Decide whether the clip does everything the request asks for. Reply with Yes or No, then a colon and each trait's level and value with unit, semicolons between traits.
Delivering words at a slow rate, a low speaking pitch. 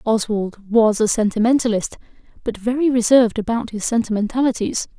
No: slow, 120 wpm; high, 225 Hz